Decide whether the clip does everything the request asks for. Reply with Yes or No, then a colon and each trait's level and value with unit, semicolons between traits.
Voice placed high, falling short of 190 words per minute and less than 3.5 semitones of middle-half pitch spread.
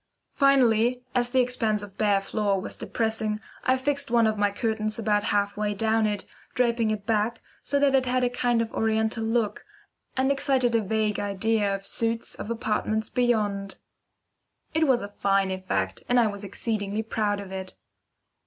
Yes: high, 220 Hz; average, 170 wpm; average, 2.9 semitones